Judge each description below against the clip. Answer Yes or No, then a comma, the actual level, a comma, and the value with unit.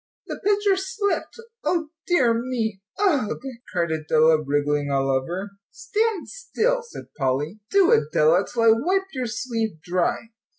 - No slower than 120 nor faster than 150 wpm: Yes, average, 140 wpm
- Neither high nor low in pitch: No, high, 225 Hz